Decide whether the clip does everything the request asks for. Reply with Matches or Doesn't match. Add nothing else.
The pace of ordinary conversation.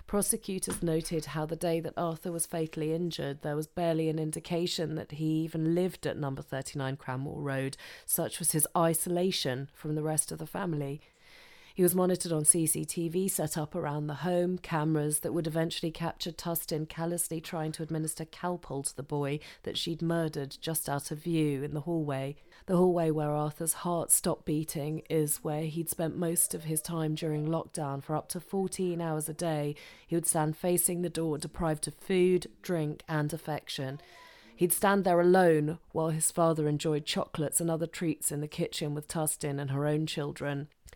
Matches